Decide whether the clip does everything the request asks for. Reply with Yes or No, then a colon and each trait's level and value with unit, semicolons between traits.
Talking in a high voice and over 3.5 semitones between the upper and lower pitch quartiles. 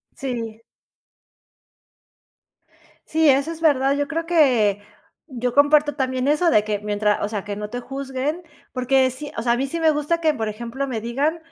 Yes: very high, 265 Hz; average, 4.5 semitones